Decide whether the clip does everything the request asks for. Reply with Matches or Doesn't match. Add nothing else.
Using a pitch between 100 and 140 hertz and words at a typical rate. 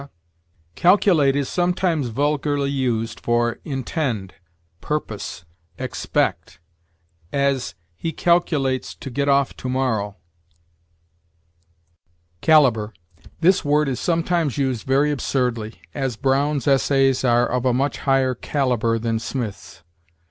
Doesn't match